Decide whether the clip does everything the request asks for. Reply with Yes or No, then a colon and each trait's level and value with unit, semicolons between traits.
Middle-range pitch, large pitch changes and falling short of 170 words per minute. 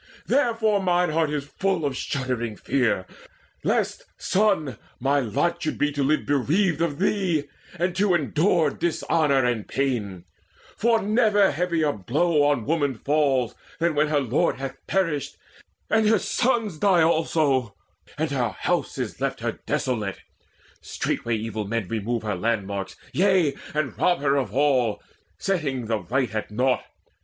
Yes: medium, 145 Hz; wide, 6.1 semitones; average, 150 wpm